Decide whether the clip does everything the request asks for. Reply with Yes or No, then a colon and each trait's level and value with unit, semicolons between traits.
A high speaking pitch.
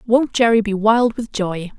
Yes: high, 220 Hz